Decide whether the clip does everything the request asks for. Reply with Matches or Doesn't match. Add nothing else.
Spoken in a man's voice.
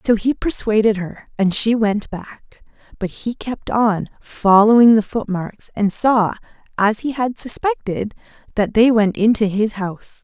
Doesn't match